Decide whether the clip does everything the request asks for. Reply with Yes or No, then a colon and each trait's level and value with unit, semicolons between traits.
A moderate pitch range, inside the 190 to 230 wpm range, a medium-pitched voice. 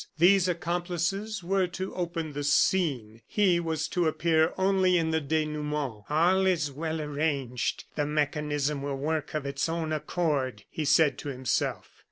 No: average, 3.2 semitones; average, 155 wpm; medium, 160 Hz